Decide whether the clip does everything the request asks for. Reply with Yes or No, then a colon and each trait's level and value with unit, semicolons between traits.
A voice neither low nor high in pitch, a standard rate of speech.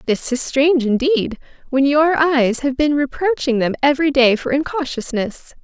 No: very high, 275 Hz; average, 160 wpm